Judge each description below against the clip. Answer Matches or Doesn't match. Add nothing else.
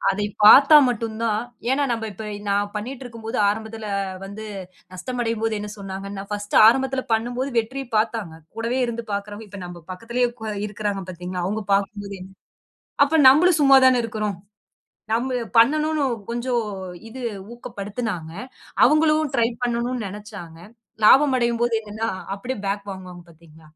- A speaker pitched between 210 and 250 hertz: Matches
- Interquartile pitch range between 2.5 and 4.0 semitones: Matches